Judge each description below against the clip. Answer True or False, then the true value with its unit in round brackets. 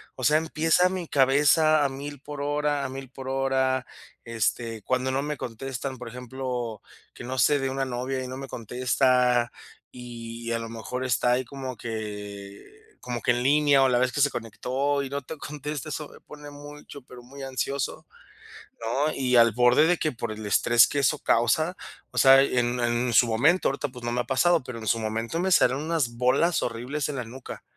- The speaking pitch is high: False (130 Hz)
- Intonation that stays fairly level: False (3.1 semitones)